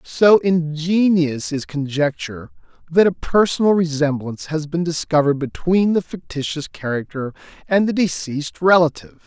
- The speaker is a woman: No, male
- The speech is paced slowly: Yes, slow, 125 wpm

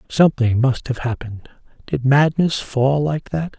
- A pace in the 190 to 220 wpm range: No, average, 150 wpm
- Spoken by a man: Yes, male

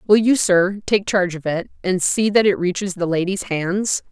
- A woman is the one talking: Yes, female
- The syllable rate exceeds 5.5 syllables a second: No, 4.9 syllables/s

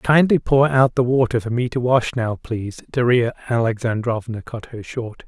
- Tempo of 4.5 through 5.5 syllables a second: Yes, 4.8 syllables/s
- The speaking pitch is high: No, low, 120 Hz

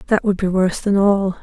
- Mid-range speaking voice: No, high, 195 Hz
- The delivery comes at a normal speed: No, fast, 255 wpm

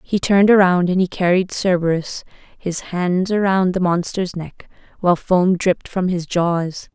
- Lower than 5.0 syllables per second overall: Yes, 4.5 syllables/s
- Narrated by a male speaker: No, female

